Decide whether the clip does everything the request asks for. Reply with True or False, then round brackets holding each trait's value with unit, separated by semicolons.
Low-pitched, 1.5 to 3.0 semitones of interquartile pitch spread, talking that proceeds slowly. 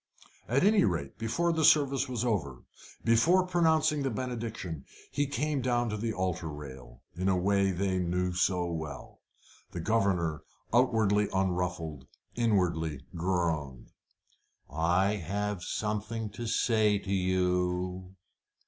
False (95 Hz; 4.8 semitones; 125 wpm)